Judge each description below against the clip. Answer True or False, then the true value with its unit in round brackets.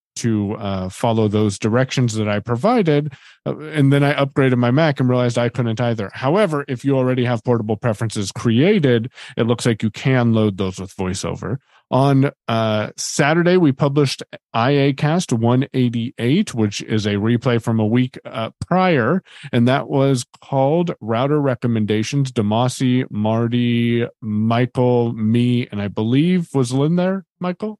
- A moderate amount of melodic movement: True (3.7 semitones)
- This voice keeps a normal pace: True (150 wpm)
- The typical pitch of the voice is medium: False (125 Hz)